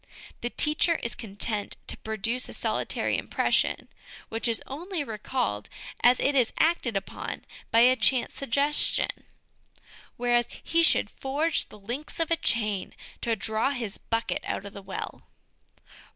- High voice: Yes, high, 240 Hz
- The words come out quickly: No, average, 150 wpm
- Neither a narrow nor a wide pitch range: Yes, average, 4.4 semitones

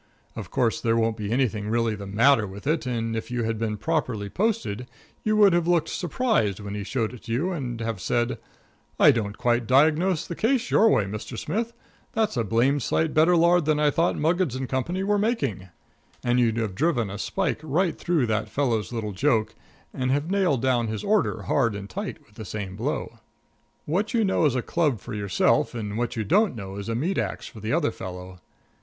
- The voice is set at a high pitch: No, low, 125 Hz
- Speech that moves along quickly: Yes, fast, 210 wpm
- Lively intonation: Yes, wide, 7.1 semitones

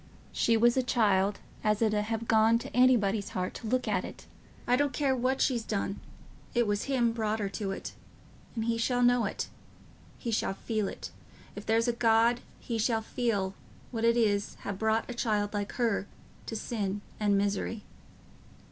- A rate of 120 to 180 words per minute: No, average, 190 wpm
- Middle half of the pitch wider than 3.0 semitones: No, narrow, 2.6 semitones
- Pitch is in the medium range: No, high, 225 Hz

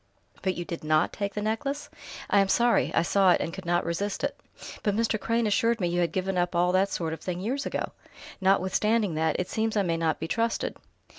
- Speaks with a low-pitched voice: No, high, 190 Hz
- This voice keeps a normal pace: No, fast, 230 wpm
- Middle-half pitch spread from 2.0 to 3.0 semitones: No, average, 4.0 semitones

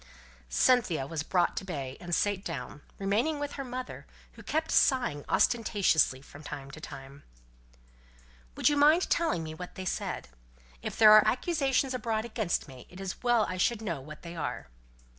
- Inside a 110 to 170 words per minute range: No, average, 180 wpm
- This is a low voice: No, high, 195 Hz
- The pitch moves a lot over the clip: Yes, wide, 8.4 semitones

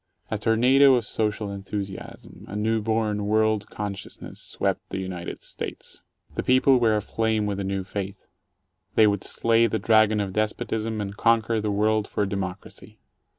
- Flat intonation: Yes, narrow, 1.9 semitones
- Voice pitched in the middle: No, low, 105 Hz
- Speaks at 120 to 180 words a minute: Yes, average, 155 wpm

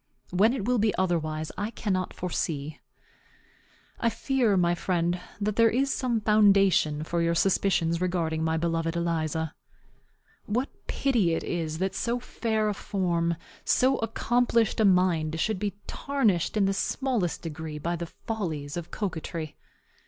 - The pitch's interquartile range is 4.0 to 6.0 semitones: Yes, average, 4.8 semitones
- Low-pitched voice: No, medium, 185 Hz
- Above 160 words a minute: No, average, 145 wpm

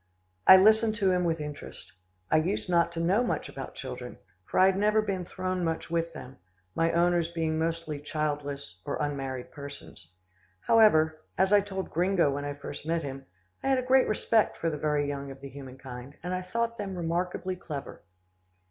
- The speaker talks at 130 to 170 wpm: No, average, 190 wpm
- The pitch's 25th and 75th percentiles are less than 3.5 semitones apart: No, average, 4.6 semitones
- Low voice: No, medium, 165 Hz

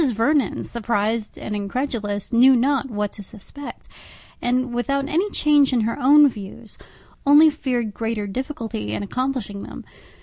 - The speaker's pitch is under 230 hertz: No, high, 240 Hz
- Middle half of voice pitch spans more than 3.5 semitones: Yes, average, 4.8 semitones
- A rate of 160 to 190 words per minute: No, average, 140 wpm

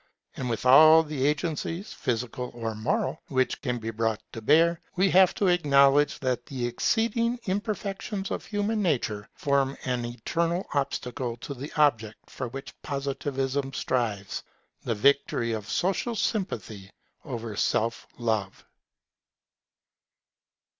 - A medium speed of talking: No, slow, 130 wpm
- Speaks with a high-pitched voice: No, low, 135 Hz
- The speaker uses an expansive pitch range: Yes, wide, 6.2 semitones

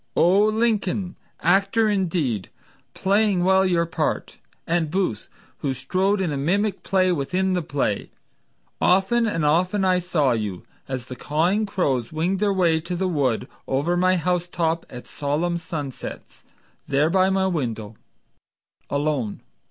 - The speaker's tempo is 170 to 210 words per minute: No, average, 140 wpm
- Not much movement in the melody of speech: No, average, 4.8 semitones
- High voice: No, medium, 175 Hz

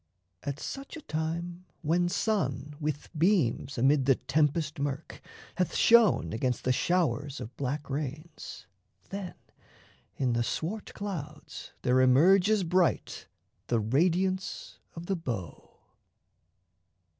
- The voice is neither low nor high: Yes, medium, 155 Hz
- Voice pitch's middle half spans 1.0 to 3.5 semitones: No, average, 5.2 semitones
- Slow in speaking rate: Yes, slow, 115 wpm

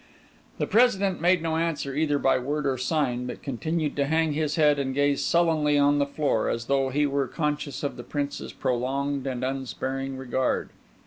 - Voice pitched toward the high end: No, medium, 145 Hz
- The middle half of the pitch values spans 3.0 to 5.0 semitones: No, narrow, 2.6 semitones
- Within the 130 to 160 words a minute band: No, average, 185 wpm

